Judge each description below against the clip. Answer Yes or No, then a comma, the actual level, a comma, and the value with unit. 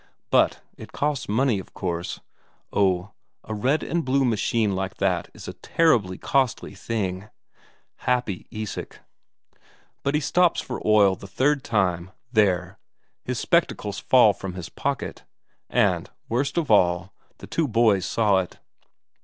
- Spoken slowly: No, average, 145 wpm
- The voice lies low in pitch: Yes, low, 105 Hz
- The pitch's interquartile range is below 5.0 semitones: No, wide, 5.5 semitones